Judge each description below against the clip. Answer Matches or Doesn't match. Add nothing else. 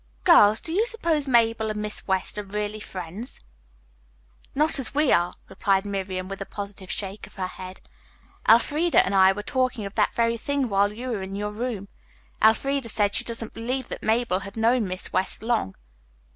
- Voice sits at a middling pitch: Doesn't match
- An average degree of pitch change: Matches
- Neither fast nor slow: Matches